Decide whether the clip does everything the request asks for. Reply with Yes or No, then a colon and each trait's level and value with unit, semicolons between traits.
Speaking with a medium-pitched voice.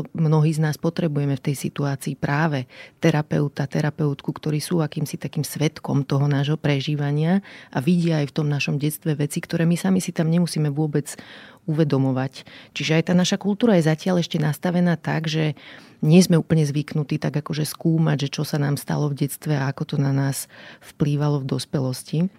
Yes: medium, 155 Hz